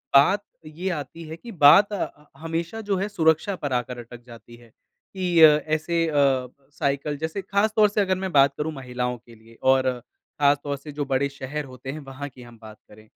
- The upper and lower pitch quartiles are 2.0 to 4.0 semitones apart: No, average, 4.4 semitones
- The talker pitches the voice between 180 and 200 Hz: No, medium, 145 Hz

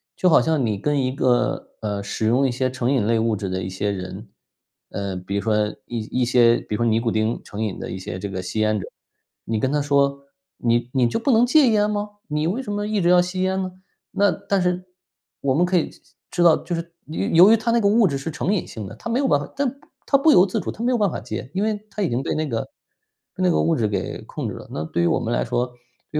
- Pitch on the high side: No, medium, 140 Hz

